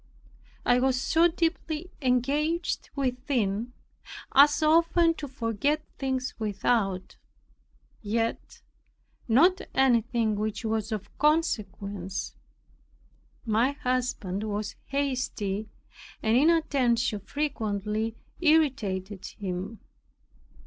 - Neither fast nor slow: No, slow, 80 wpm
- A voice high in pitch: Yes, high, 245 Hz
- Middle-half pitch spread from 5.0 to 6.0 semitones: Yes, wide, 5.4 semitones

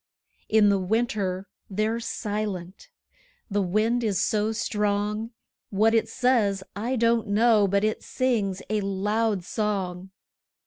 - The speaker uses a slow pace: Yes, slow, 125 wpm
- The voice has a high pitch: Yes, high, 210 Hz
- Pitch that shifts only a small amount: Yes, narrow, 2.3 semitones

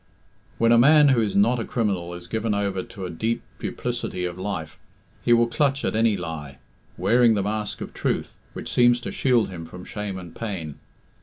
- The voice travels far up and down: No, average, 4.6 semitones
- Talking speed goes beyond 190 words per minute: Yes, average, 200 wpm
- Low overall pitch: Yes, low, 105 Hz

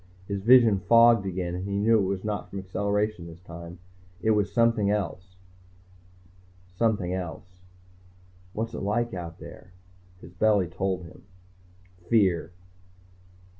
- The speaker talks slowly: Yes, slow, 130 wpm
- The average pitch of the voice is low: Yes, low, 100 Hz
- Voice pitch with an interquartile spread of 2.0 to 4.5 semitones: Yes, average, 3.0 semitones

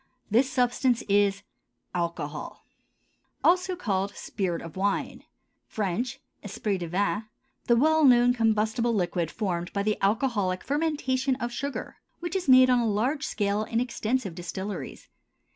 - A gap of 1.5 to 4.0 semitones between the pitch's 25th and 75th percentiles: No, average, 4.7 semitones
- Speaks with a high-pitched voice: Yes, high, 220 Hz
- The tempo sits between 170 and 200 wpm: No, slow, 135 wpm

